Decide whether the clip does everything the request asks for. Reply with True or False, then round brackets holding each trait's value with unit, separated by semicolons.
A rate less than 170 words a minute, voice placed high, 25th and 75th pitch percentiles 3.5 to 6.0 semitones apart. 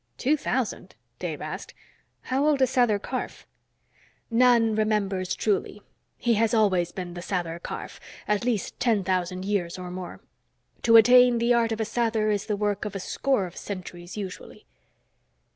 True (160 wpm; 210 Hz; 4.1 semitones)